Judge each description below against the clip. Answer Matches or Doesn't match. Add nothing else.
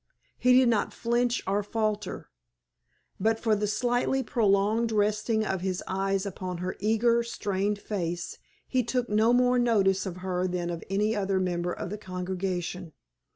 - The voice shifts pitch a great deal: Doesn't match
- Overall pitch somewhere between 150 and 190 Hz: Doesn't match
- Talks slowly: Doesn't match